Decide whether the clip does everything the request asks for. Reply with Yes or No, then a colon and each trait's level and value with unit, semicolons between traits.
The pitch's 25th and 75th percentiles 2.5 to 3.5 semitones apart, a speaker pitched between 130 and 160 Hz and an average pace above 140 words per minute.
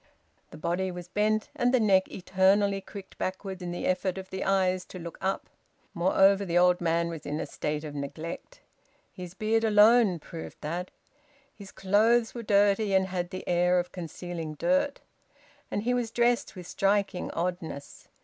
No: average, 2.8 semitones; high, 190 Hz; average, 170 wpm